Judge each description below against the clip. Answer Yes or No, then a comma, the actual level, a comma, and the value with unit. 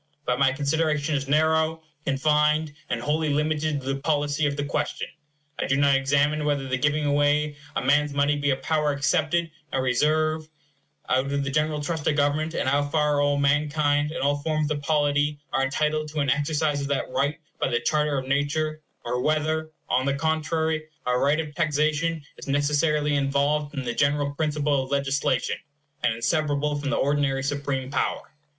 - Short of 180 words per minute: No, average, 185 wpm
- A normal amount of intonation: No, narrow, 1.5 semitones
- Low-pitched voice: No, medium, 145 Hz